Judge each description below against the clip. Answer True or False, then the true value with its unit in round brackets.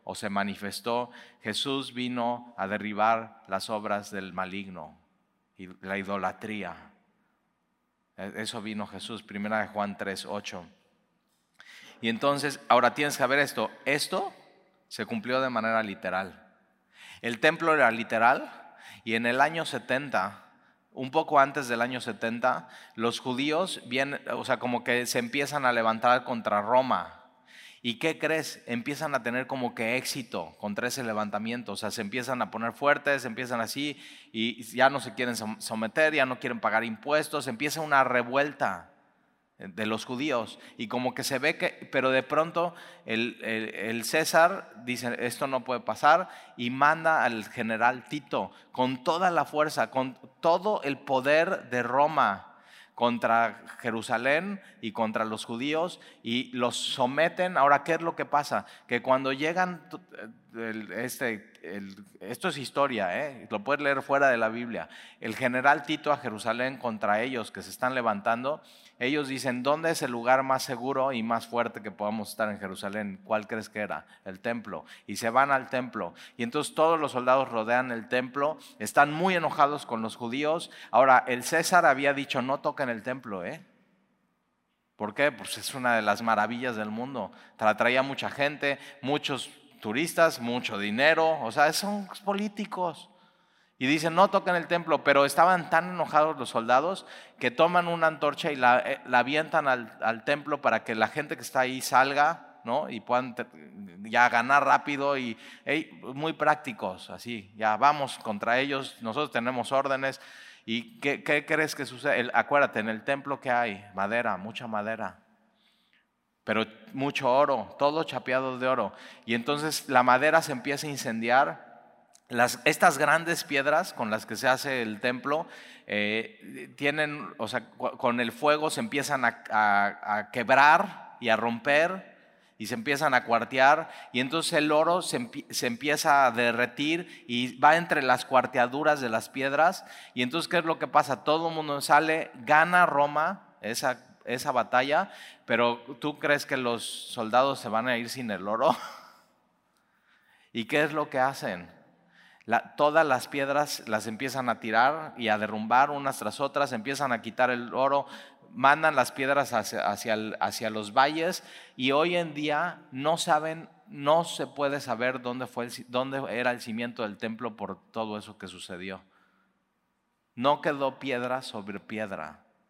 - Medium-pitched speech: False (130 Hz)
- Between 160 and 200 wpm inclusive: True (165 wpm)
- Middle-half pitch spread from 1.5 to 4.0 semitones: False (4.4 semitones)